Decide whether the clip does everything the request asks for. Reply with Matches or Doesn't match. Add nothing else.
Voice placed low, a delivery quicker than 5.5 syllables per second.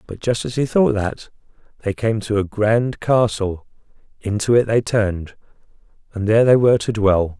Doesn't match